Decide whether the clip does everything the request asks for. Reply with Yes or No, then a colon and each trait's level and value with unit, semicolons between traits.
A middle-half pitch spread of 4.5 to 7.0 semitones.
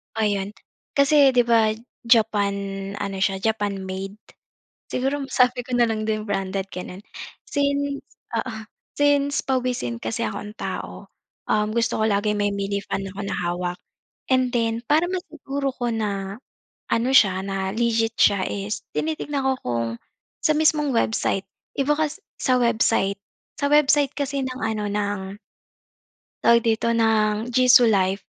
Yes: average, 4.8 semitones